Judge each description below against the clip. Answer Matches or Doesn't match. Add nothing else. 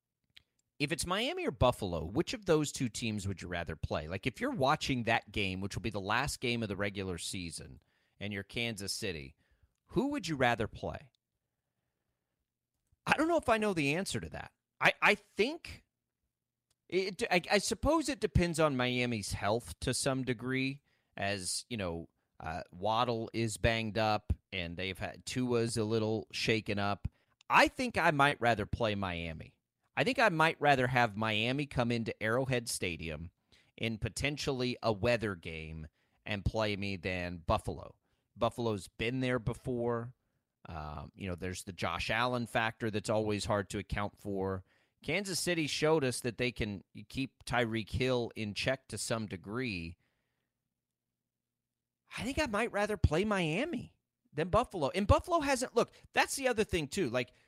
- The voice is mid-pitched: Doesn't match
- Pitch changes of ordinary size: Doesn't match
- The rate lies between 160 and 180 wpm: Matches